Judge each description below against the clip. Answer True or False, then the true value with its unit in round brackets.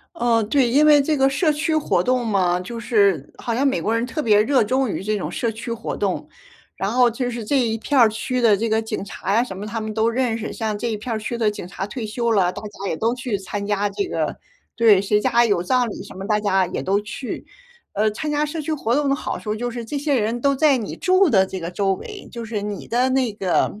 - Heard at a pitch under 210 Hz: False (230 Hz)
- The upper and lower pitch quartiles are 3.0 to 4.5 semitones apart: True (3.7 semitones)